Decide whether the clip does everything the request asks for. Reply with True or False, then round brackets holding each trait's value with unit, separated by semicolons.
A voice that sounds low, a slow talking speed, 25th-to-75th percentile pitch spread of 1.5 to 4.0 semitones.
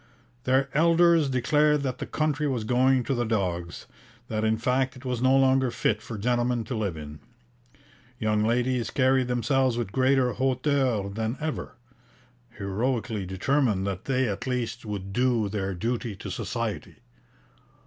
False (125 Hz; 150 wpm; 3.6 semitones)